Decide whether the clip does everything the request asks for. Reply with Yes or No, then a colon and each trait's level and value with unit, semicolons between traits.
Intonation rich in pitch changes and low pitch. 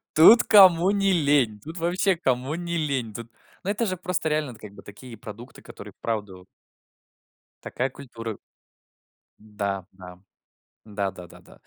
Yes: wide, 8.3 semitones; low, 130 Hz